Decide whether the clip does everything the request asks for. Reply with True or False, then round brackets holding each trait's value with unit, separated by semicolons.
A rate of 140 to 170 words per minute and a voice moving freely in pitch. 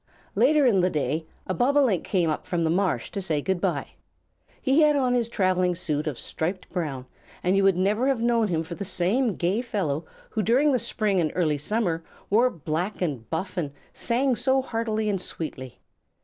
False (195 wpm; 6.0 semitones)